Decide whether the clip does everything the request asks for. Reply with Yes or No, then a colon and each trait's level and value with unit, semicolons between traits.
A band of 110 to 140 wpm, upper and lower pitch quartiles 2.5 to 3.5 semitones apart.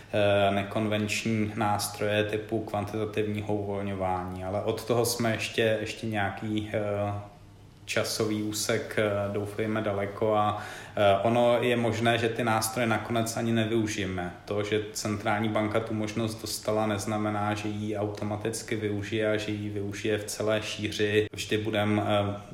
No: average, 120 wpm; narrow, 1.2 semitones